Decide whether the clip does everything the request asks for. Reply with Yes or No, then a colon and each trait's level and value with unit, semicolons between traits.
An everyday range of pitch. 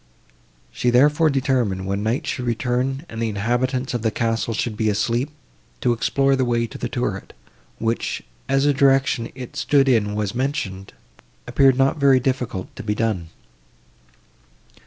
Yes: average, 3.3 semitones